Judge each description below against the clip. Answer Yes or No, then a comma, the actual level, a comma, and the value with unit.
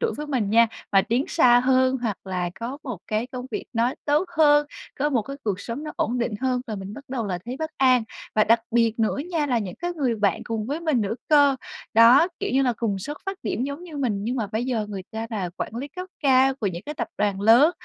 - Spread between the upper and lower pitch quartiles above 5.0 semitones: No, average, 4.6 semitones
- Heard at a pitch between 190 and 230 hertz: No, high, 245 Hz